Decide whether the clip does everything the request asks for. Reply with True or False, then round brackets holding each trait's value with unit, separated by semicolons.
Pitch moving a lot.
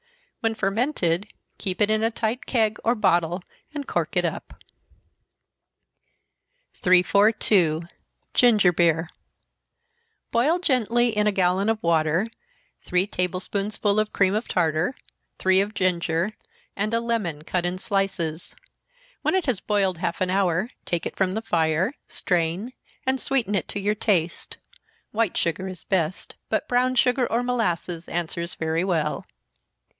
False (4.4 semitones)